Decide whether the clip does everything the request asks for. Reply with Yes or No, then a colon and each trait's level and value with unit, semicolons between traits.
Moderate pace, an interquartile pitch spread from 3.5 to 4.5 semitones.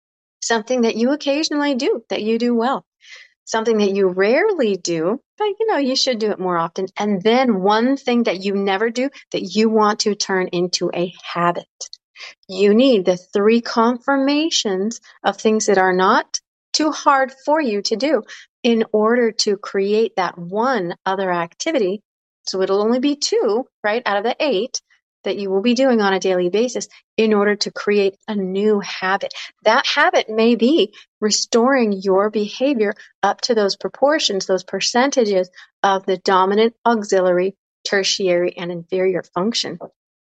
Yes: average, 165 wpm; average, 4.1 semitones